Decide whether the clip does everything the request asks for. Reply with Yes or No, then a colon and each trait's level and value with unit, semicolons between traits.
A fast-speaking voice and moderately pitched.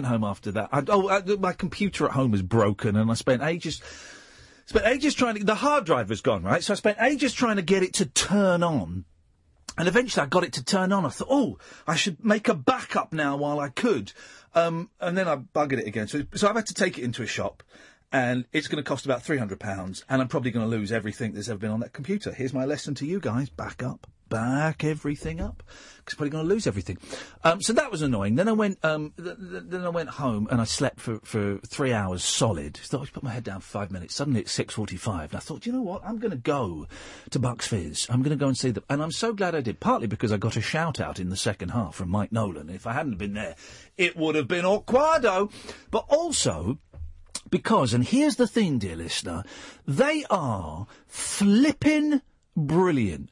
Yes: fast, 240 wpm; medium, 145 Hz